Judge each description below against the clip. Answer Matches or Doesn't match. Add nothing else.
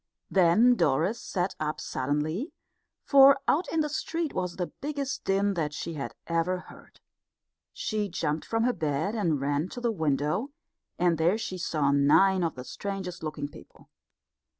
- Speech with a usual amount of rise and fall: Doesn't match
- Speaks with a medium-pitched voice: Matches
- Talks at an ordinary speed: Matches